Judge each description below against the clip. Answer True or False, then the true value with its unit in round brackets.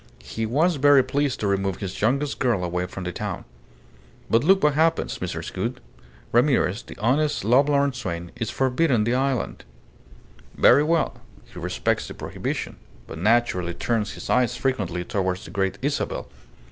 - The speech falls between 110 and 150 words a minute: False (160 wpm)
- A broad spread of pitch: True (6.4 semitones)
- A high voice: False (120 Hz)